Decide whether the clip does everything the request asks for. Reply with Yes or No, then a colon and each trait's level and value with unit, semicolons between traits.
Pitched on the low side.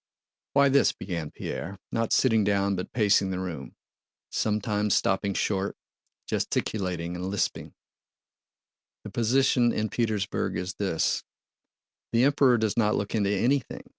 Yes: low, 105 Hz